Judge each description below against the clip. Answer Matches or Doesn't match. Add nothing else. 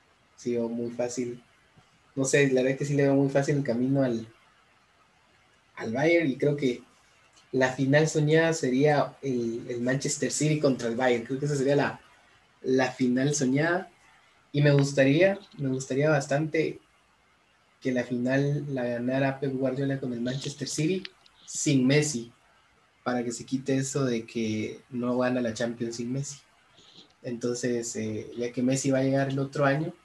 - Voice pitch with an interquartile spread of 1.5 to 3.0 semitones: Matches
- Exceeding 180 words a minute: Doesn't match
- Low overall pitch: Matches